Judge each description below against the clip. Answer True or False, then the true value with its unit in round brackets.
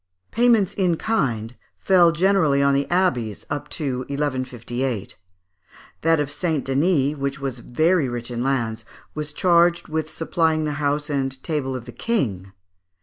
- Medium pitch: True (145 Hz)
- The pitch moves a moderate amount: True (4.4 semitones)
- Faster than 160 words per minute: False (145 wpm)